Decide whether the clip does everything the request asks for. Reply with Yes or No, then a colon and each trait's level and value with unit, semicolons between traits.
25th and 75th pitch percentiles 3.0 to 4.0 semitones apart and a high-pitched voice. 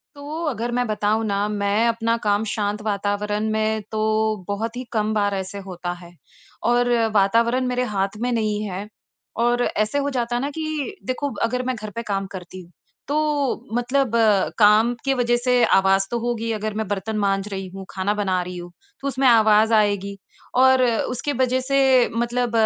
Yes: average, 3.3 semitones; high, 220 Hz